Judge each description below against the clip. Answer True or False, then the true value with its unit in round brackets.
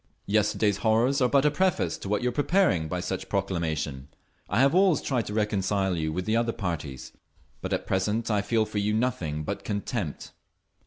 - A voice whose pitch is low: True (105 Hz)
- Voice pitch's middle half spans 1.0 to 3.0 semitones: False (4.6 semitones)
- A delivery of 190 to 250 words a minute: True (200 wpm)